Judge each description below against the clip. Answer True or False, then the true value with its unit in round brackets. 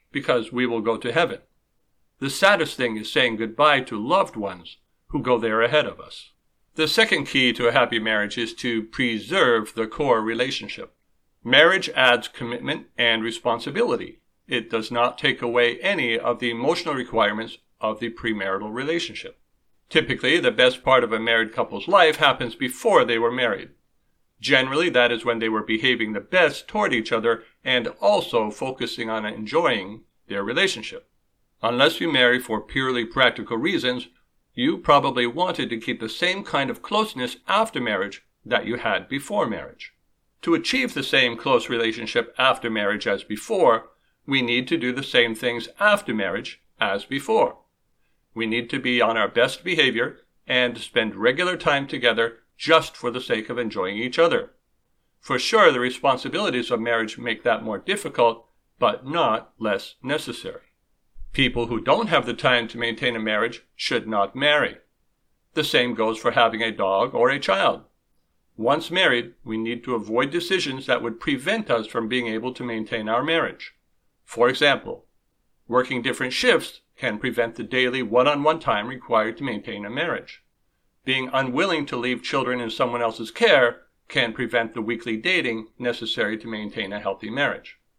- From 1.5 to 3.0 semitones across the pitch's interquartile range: True (2.7 semitones)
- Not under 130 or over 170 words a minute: True (165 wpm)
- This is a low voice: True (120 Hz)